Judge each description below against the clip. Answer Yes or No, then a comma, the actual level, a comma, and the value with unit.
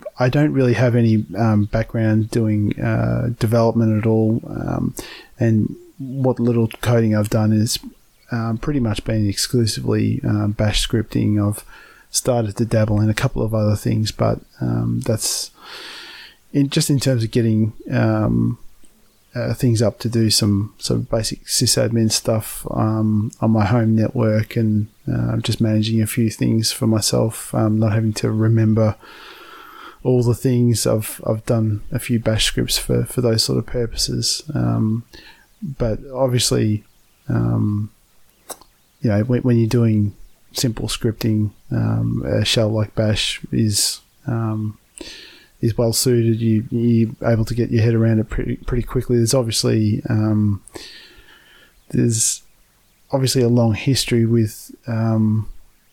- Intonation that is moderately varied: No, narrow, 1.9 semitones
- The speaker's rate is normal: Yes, average, 145 wpm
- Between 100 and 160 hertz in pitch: Yes, low, 110 Hz